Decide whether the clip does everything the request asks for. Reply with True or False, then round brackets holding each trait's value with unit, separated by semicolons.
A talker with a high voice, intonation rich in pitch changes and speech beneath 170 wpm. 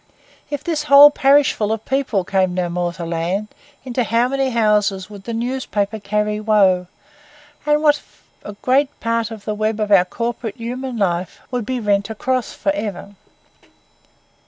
False (215 Hz; 4.2 semitones; 160 wpm)